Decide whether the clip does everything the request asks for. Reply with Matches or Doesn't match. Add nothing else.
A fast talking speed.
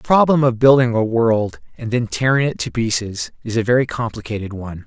Matches